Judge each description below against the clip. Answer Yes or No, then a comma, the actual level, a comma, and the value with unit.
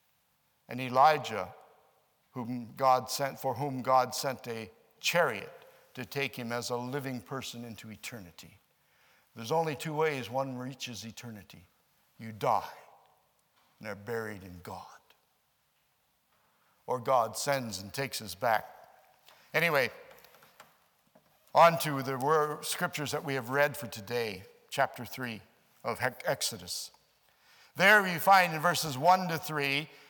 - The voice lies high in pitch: No, low, 130 Hz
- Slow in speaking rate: Yes, slow, 130 wpm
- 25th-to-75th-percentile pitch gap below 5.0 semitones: Yes, average, 4.1 semitones